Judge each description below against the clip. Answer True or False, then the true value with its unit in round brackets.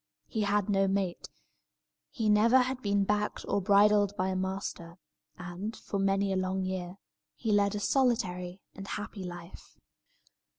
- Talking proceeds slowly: False (160 wpm)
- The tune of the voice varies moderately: False (1.9 semitones)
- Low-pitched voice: False (200 Hz)